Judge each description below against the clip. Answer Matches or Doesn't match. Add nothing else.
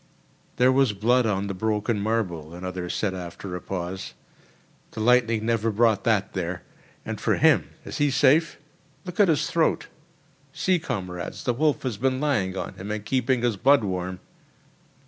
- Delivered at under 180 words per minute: Matches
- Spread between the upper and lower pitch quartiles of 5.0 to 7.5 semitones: Matches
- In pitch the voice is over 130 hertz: Doesn't match